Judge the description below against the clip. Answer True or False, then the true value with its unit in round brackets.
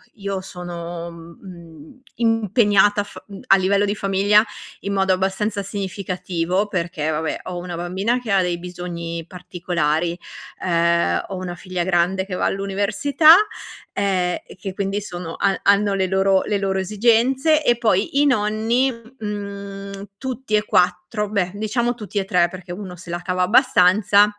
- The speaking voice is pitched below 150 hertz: False (195 Hz)